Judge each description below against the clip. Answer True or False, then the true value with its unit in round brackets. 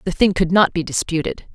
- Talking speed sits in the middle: False (235 wpm)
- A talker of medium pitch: True (175 Hz)